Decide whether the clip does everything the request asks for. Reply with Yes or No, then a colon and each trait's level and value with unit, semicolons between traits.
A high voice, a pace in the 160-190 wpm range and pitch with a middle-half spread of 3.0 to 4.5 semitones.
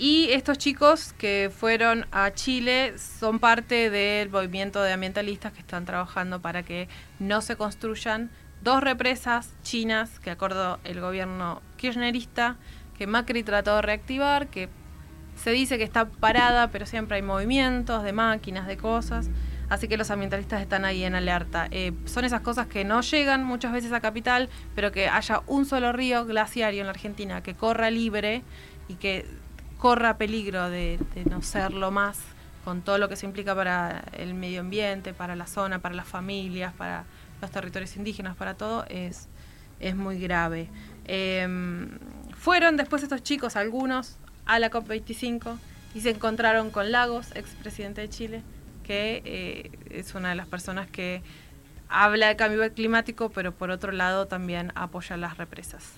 Yes: high, 210 Hz; average, 165 wpm; average, 3.9 semitones